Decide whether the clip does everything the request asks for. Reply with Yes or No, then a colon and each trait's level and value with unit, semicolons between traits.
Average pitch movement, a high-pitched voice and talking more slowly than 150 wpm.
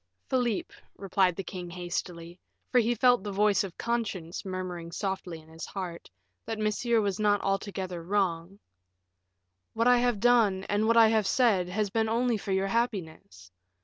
No: average, 3.8 semitones; high, 195 Hz; average, 165 wpm